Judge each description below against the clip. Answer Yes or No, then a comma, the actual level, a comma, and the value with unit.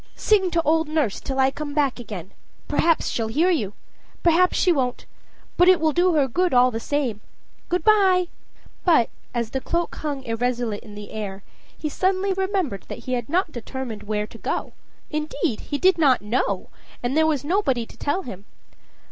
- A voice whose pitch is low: No, very high, 285 Hz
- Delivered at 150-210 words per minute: Yes, average, 180 wpm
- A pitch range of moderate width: No, wide, 6.6 semitones